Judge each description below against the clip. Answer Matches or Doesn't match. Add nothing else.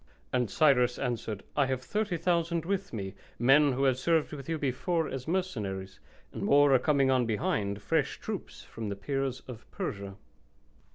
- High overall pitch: Doesn't match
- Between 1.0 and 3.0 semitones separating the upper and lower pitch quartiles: Doesn't match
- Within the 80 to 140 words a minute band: Doesn't match